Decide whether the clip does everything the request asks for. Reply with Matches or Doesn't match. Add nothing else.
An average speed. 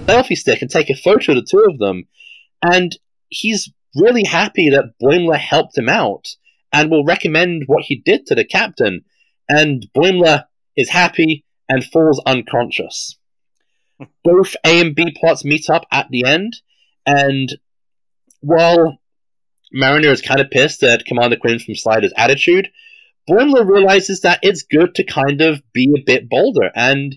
Matches